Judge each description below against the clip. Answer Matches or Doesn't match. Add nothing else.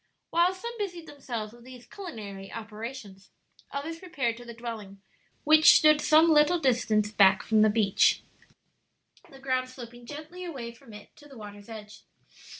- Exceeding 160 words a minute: Doesn't match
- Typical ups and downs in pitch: Doesn't match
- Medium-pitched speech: Doesn't match